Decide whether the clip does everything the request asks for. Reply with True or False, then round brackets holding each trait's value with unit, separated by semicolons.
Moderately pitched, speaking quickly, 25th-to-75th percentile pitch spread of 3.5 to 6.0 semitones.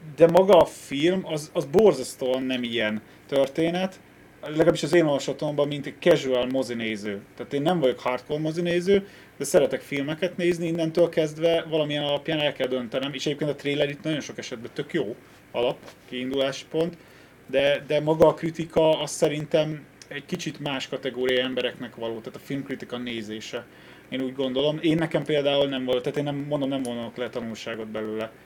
True (145 Hz; 175 wpm; 3.8 semitones)